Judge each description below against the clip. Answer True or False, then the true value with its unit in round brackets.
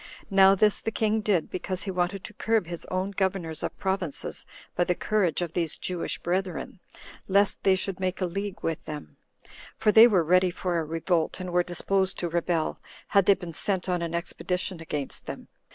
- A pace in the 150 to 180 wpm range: False (195 wpm)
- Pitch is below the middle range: False (185 Hz)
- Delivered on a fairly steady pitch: True (2.3 semitones)